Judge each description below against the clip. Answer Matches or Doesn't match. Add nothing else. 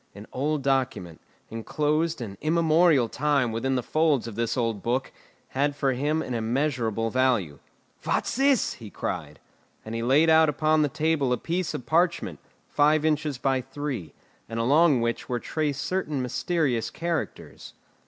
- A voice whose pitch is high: Doesn't match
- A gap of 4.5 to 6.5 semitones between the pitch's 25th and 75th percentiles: Matches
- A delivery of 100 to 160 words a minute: Matches